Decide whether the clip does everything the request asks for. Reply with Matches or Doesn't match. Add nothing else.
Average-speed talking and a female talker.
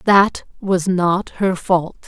Matches